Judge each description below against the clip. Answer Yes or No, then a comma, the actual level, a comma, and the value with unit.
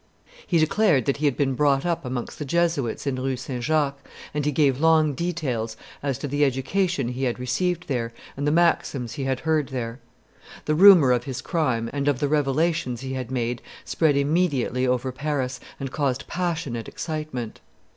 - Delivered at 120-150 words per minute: No, average, 185 wpm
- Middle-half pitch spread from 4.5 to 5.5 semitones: No, average, 3.6 semitones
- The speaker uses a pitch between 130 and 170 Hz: Yes, medium, 140 Hz